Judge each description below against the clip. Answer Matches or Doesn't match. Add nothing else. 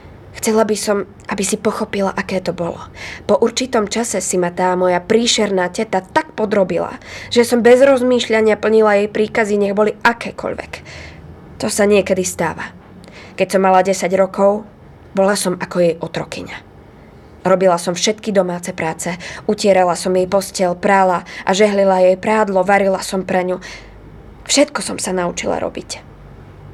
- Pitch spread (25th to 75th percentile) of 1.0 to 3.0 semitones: Matches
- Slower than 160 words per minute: Matches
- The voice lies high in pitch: Matches